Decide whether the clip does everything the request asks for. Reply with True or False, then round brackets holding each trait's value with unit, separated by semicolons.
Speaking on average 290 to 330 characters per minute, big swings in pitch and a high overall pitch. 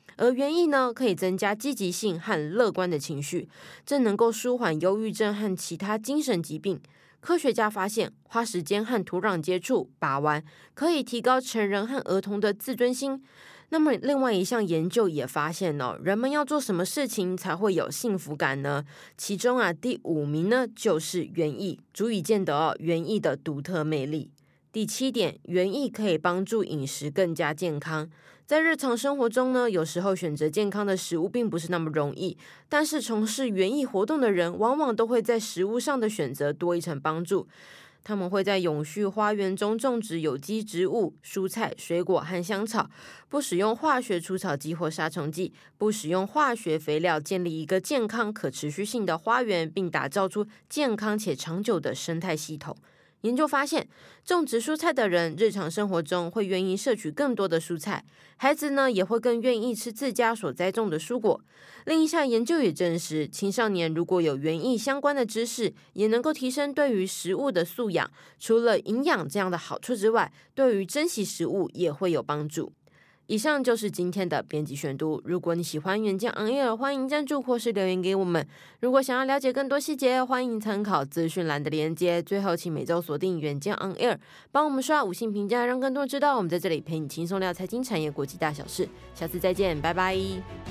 True (295 characters per minute; 6.2 semitones; 195 Hz)